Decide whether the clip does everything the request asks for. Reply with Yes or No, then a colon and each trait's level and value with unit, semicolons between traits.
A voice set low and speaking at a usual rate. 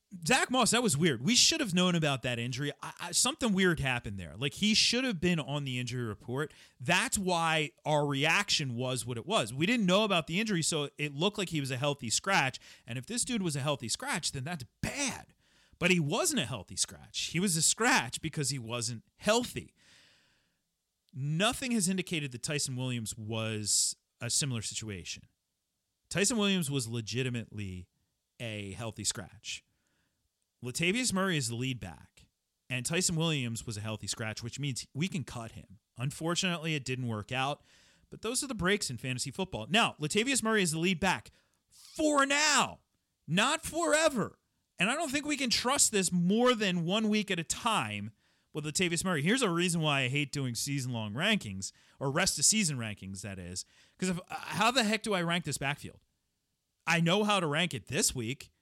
No: medium, 155 Hz; average, 190 wpm